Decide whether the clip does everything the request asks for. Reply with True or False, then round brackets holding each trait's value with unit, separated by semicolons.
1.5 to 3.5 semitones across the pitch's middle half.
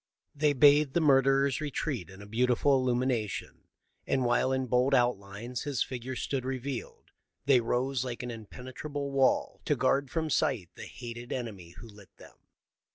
True (2.6 semitones)